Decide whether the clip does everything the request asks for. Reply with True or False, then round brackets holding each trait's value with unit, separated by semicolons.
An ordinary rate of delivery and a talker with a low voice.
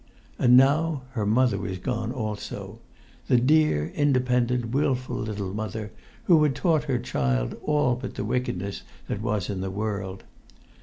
True (155 wpm; 120 Hz)